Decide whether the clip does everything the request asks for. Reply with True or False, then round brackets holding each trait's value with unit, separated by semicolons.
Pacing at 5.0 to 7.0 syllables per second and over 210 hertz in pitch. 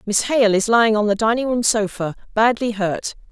True (5.2 syllables/s; 220 Hz)